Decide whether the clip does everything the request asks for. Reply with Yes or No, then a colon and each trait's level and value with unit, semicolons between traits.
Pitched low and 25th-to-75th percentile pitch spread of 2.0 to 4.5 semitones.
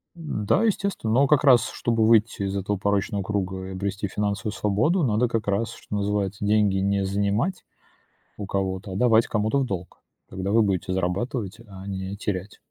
Yes: low, 100 Hz; narrow, 2.6 semitones